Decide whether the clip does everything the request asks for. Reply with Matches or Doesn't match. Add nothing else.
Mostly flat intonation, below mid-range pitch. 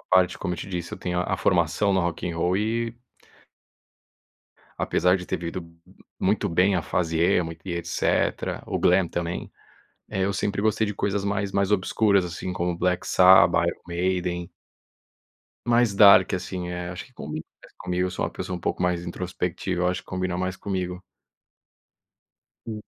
Matches